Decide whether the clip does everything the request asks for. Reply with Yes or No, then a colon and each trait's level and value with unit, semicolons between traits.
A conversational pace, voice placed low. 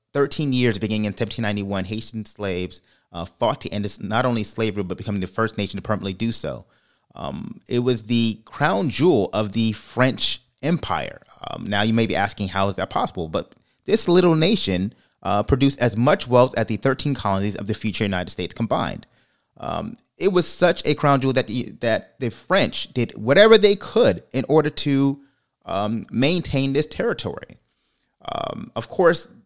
Yes: average, 180 wpm; low, 115 Hz